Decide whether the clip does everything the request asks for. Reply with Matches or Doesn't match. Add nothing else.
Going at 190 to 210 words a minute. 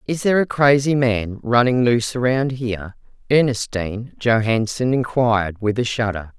Doesn't match